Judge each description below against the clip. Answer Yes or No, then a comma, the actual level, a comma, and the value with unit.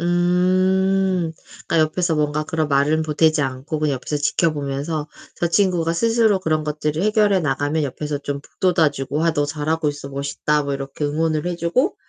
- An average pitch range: Yes, average, 3.1 semitones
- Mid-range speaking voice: Yes, medium, 155 Hz